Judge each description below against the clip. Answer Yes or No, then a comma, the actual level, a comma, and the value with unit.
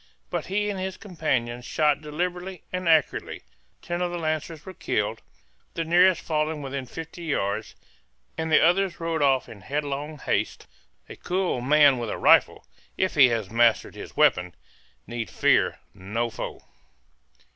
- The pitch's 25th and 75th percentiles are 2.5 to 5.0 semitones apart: No, wide, 5.4 semitones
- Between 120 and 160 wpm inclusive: Yes, average, 155 wpm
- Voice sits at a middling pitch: Yes, medium, 155 Hz